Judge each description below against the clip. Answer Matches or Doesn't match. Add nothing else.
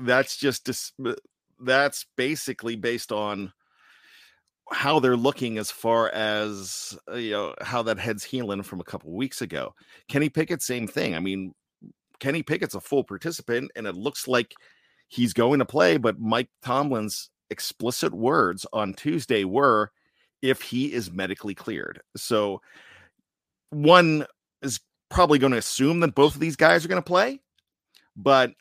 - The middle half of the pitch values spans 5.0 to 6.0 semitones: Matches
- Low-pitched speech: Matches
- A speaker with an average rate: Matches